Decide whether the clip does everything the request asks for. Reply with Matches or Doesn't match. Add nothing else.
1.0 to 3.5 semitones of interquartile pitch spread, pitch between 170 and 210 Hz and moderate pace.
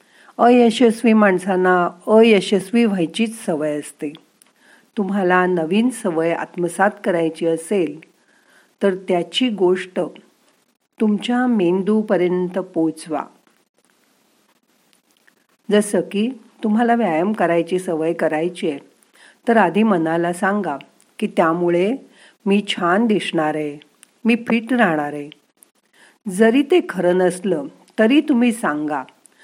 Doesn't match